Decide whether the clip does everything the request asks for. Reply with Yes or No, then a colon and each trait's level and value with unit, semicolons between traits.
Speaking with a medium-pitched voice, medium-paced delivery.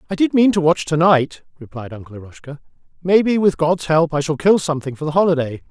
No: medium, 160 Hz; fast, 210 wpm